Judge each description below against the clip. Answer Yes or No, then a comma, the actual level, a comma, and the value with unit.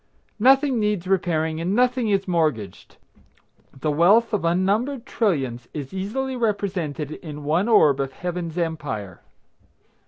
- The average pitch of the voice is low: No, medium, 180 Hz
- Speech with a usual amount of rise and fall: No, wide, 5.8 semitones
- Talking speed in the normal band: No, slow, 125 wpm